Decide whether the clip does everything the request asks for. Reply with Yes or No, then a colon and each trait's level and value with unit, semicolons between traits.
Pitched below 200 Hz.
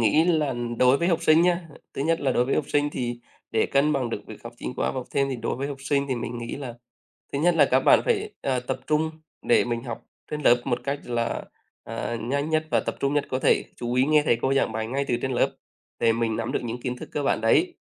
Yes: low, 135 Hz